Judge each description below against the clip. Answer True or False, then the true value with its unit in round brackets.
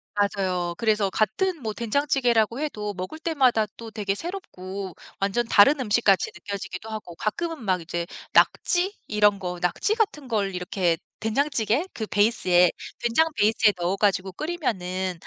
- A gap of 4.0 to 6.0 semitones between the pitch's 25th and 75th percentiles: True (5.1 semitones)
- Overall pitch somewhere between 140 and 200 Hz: False (210 Hz)